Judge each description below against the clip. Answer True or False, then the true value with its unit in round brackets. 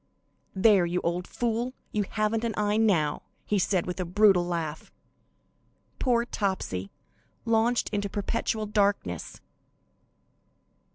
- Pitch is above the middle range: True (205 Hz)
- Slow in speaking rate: True (115 wpm)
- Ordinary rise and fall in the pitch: True (3.8 semitones)